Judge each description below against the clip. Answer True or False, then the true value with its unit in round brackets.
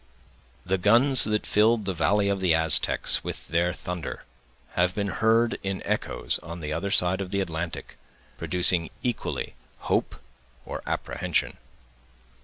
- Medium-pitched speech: False (95 Hz)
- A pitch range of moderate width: True (3.2 semitones)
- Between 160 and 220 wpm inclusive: False (140 wpm)